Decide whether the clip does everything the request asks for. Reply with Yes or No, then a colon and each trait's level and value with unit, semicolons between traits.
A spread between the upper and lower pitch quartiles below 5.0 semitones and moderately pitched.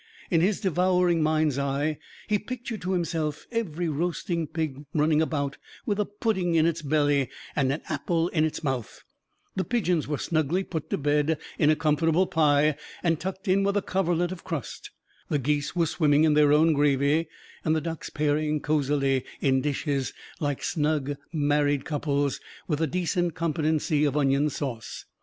Yes: average, 2.9 semitones; medium, 155 Hz